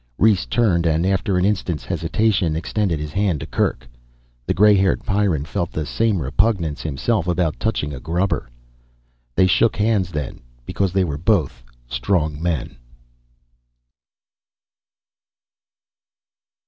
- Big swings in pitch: No, average, 4.6 semitones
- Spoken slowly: Yes, slow, 125 wpm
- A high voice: No, very low, 90 Hz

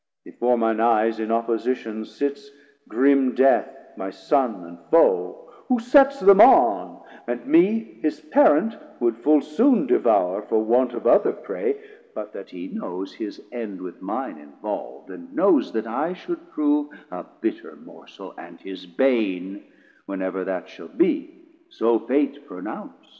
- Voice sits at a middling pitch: No, low, 130 Hz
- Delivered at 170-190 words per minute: No, average, 150 wpm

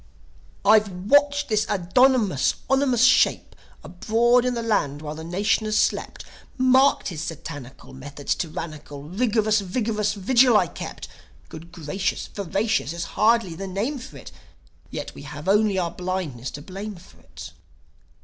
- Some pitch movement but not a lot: No, wide, 5.7 semitones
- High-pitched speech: Yes, high, 200 Hz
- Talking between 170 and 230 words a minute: No, average, 145 wpm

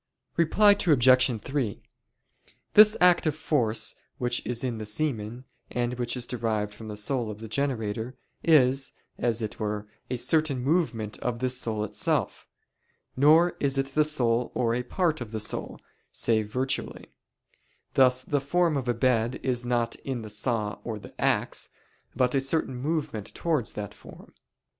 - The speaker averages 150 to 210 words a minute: Yes, average, 160 wpm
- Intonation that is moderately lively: Yes, average, 3.9 semitones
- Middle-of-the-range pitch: No, low, 125 Hz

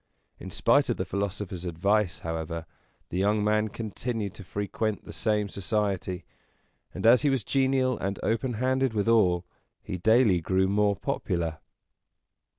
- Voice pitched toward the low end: Yes, low, 105 Hz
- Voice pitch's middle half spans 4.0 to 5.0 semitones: No, average, 3.3 semitones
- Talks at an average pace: Yes, average, 150 wpm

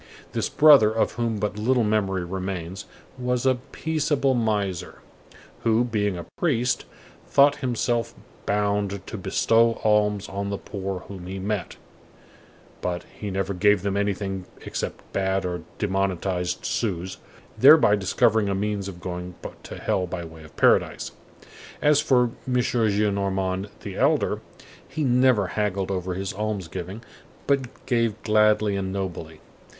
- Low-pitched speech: Yes, low, 100 Hz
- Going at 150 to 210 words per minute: No, average, 140 wpm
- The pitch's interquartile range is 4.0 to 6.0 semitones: No, average, 3.4 semitones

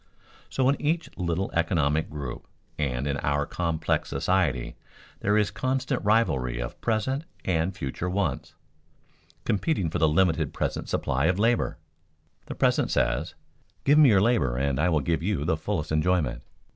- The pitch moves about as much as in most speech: No, wide, 6.2 semitones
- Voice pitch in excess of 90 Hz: No, very low, 85 Hz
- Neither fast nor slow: Yes, average, 155 wpm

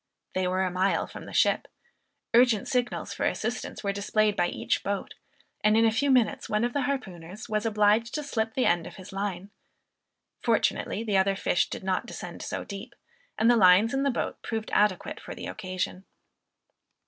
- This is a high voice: Yes, high, 210 Hz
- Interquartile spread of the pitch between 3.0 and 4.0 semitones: Yes, average, 3.3 semitones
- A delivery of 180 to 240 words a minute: Yes, average, 190 wpm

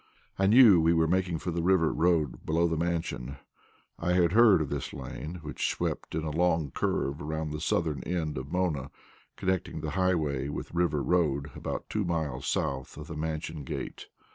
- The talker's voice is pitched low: Yes, very low, 80 Hz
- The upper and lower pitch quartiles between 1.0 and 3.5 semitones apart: Yes, average, 2.8 semitones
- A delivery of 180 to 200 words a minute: Yes, average, 185 wpm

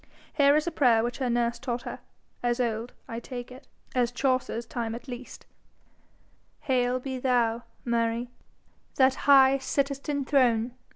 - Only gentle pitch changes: Yes, narrow, 2.1 semitones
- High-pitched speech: Yes, very high, 250 Hz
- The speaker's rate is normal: Yes, average, 155 wpm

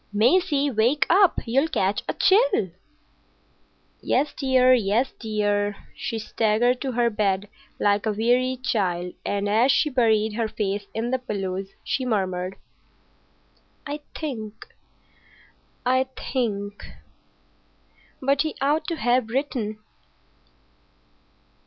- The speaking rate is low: Yes, slow, 110 wpm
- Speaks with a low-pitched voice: No, high, 230 Hz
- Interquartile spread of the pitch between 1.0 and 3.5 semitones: No, average, 4.2 semitones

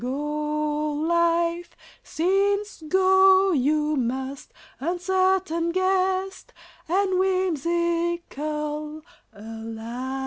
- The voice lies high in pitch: Yes, very high, 335 Hz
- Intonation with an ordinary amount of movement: Yes, average, 4.0 semitones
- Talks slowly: Yes, slow, 65 wpm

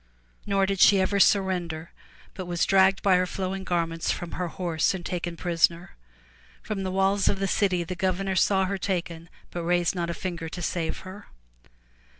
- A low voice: No, medium, 185 Hz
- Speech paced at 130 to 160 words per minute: No, average, 180 wpm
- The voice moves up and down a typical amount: No, narrow, 2.0 semitones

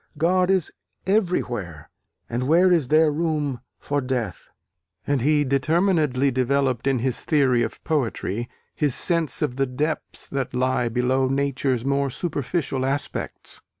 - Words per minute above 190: No, slow, 135 wpm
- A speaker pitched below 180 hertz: Yes, medium, 140 Hz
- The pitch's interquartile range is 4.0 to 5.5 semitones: No, average, 3.4 semitones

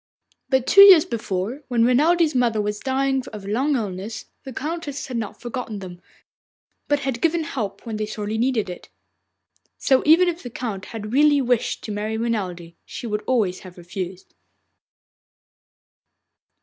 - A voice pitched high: Yes, high, 235 Hz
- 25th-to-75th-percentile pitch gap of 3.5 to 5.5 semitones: Yes, average, 4.7 semitones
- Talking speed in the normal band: Yes, average, 160 wpm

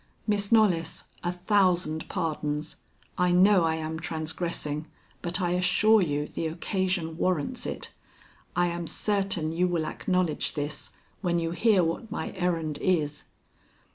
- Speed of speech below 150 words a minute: Yes, average, 140 wpm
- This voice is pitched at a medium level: Yes, medium, 175 Hz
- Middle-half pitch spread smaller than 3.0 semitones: Yes, narrow, 2.6 semitones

